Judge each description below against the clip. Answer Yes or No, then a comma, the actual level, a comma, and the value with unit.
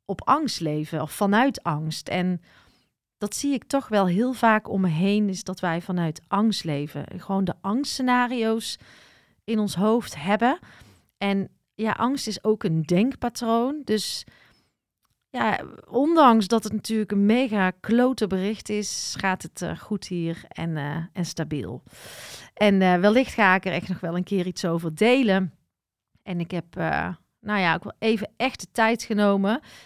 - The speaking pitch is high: Yes, high, 200 Hz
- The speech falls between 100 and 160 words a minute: No, average, 170 wpm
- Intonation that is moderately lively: Yes, average, 4.2 semitones